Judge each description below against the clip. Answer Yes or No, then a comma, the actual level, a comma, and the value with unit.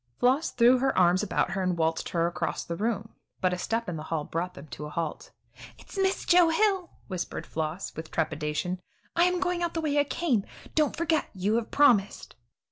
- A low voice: No, high, 205 Hz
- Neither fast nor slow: No, fast, 210 wpm